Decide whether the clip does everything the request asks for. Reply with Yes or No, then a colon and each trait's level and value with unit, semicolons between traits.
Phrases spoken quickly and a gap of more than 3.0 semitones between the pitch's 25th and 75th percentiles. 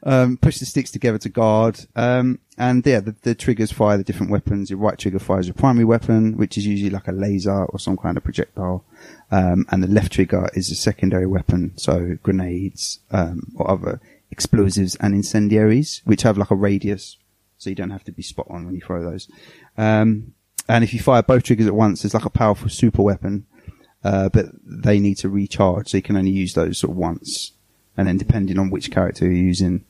No: fast, 220 wpm; average, 2.7 semitones